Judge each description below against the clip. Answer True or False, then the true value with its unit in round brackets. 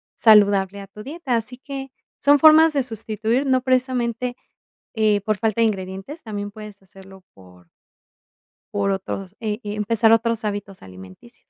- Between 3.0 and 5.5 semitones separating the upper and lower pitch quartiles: True (4.0 semitones)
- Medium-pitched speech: False (215 Hz)